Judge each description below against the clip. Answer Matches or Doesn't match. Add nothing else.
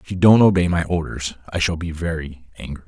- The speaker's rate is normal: Doesn't match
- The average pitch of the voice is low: Matches